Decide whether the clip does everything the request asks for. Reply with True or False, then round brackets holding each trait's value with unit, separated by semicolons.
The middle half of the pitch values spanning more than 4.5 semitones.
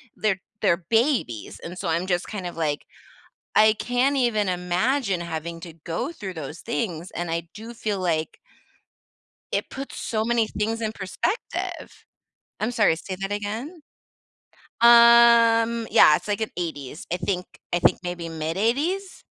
True (5.2 semitones)